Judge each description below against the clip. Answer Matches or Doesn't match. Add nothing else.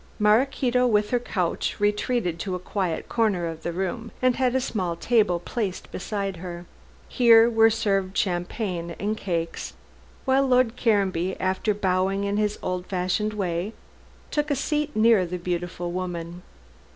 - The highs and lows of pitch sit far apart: Doesn't match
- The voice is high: Matches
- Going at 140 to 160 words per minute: Matches